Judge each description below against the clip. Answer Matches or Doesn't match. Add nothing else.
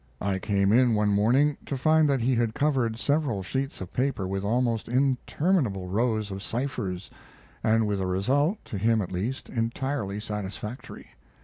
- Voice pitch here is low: Matches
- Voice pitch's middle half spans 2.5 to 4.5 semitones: Doesn't match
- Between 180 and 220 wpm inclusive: Doesn't match